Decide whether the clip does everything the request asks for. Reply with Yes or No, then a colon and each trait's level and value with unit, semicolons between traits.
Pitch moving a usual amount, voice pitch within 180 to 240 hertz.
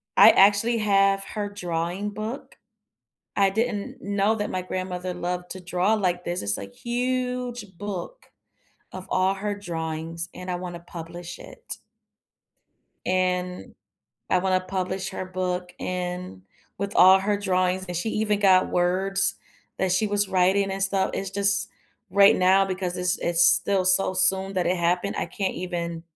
No: narrow, 2.0 semitones; medium, 185 Hz